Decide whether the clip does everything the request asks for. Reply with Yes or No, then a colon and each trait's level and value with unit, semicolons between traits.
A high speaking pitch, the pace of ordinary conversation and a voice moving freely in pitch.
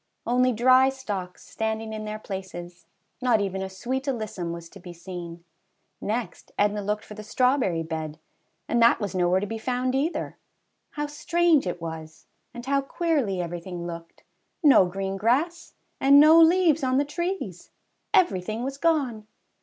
Yes: high, 220 Hz; average, 165 wpm; wide, 6.6 semitones